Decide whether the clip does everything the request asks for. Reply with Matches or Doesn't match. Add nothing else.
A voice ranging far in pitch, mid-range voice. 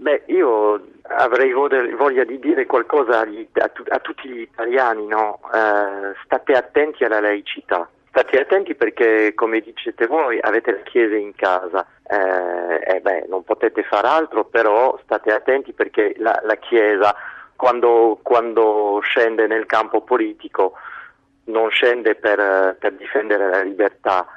Doesn't match